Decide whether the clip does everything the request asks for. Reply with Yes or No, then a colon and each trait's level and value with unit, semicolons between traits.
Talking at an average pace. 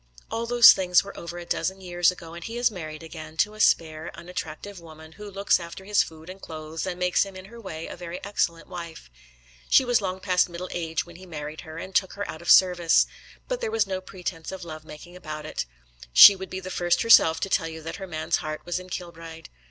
No: fast, 240 wpm